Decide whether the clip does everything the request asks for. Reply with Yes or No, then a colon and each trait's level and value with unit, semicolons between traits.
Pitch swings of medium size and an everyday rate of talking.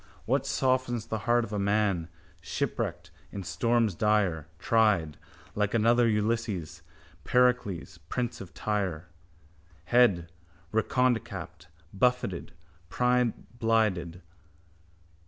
No: average, 4.3 semitones; slow, 90 wpm